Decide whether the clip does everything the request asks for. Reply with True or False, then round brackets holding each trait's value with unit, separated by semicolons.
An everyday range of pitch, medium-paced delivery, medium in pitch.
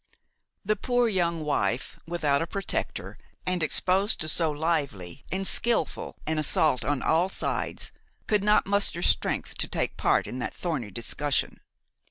True (4.8 semitones; 150 wpm; 165 Hz)